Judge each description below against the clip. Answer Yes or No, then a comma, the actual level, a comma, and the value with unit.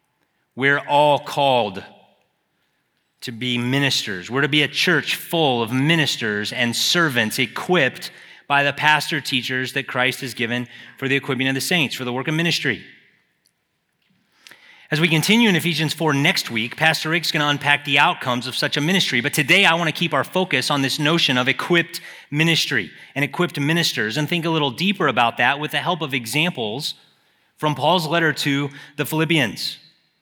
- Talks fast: No, average, 180 wpm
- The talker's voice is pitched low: No, medium, 145 Hz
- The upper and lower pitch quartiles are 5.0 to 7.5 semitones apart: No, average, 3.7 semitones